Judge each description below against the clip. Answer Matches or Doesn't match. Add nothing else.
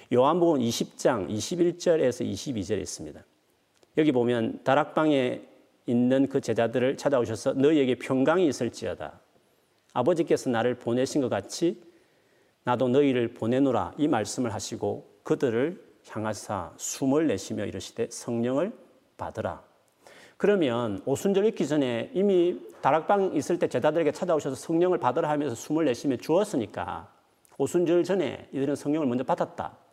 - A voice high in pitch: Doesn't match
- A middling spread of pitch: Doesn't match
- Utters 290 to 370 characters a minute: Matches